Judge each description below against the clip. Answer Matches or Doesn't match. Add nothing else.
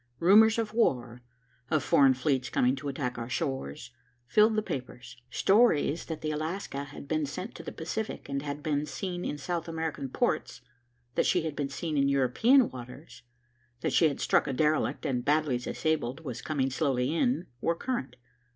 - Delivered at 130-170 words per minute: Doesn't match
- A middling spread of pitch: Matches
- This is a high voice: Doesn't match